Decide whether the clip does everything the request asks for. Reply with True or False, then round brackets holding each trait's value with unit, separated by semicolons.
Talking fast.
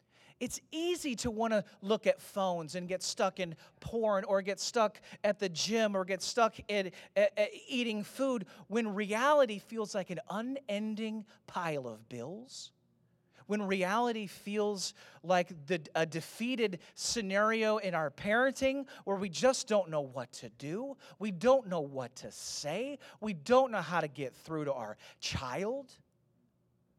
False (160 wpm)